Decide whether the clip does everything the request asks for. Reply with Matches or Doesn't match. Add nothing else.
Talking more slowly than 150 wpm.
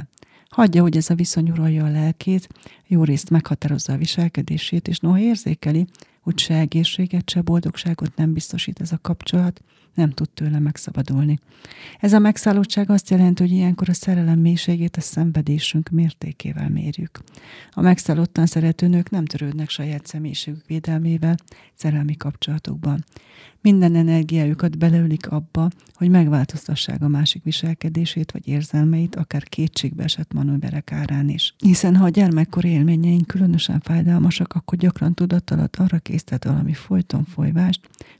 Matches